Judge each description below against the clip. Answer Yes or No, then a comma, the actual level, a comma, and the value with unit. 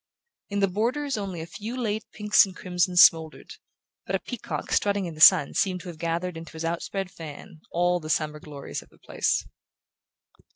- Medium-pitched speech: Yes, medium, 180 Hz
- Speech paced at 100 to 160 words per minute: No, average, 195 wpm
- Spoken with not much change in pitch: No, average, 3.7 semitones